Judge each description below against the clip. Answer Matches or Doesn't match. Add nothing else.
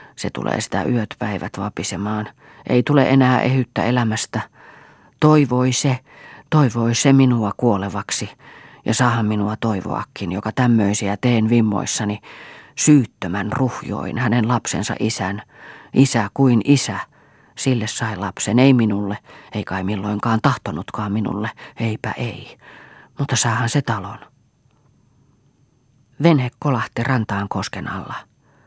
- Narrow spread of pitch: Doesn't match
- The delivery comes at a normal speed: Matches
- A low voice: Matches